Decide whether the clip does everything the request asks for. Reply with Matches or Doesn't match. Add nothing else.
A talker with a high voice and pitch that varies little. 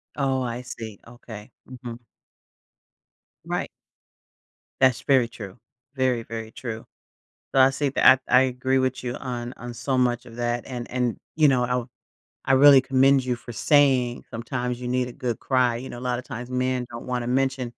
Doesn't match